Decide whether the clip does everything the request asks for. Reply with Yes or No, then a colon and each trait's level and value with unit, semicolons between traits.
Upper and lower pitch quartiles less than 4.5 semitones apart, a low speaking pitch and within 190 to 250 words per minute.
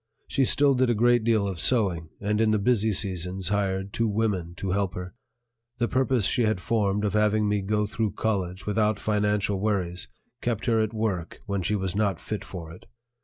Yes: narrow, 2.5 semitones; low, 105 Hz; average, 200 wpm